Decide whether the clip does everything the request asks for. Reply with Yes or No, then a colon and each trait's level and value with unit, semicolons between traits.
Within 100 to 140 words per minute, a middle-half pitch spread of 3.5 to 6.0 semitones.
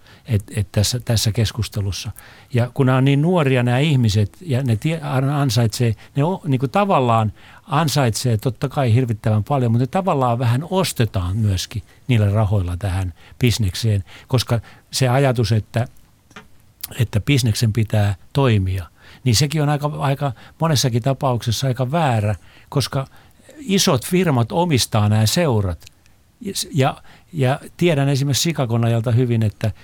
Yes: average, 135 wpm; average, 4.5 semitones